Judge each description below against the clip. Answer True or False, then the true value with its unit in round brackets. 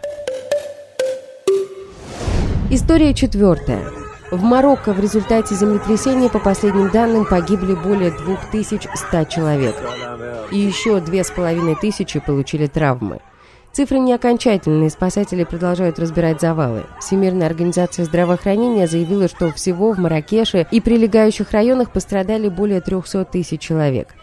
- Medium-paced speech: False (105 wpm)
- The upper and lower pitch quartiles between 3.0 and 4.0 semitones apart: False (4.7 semitones)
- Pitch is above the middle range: True (195 Hz)